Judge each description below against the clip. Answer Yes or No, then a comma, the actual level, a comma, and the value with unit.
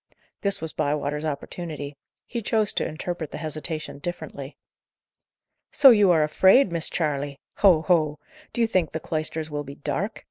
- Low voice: No, medium, 155 Hz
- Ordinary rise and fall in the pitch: Yes, average, 3.4 semitones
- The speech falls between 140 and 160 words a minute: Yes, average, 155 wpm